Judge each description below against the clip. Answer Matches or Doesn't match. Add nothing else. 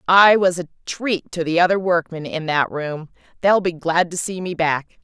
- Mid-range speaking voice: Matches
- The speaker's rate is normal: Doesn't match